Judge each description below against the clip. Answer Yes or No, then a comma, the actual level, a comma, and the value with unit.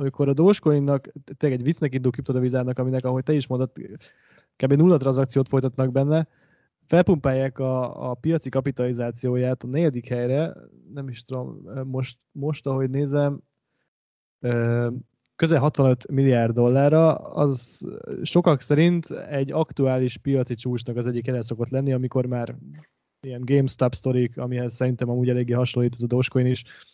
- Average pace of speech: Yes, average, 140 wpm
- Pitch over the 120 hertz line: Yes, low, 130 Hz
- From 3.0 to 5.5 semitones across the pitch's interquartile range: No, narrow, 2.5 semitones